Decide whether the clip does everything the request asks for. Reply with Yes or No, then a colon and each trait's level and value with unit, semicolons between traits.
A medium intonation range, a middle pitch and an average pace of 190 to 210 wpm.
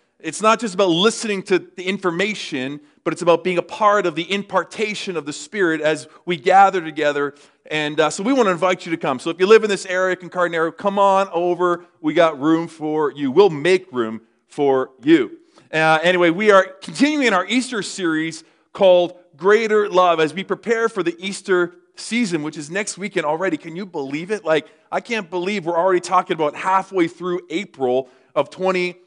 Yes: average, 3.7 semitones; medium, 180 Hz; average, 195 wpm